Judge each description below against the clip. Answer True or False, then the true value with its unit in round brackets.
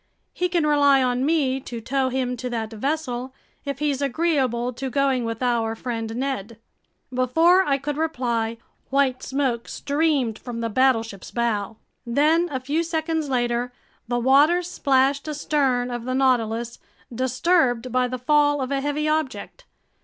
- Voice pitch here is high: True (260 Hz)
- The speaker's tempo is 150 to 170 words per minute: True (155 wpm)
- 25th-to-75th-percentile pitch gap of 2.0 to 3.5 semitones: True (3.2 semitones)